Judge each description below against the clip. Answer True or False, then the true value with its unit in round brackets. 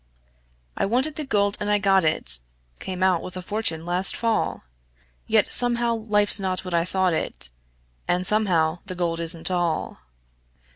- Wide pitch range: False (3.3 semitones)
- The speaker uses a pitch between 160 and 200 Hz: True (185 Hz)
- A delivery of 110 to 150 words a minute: False (160 wpm)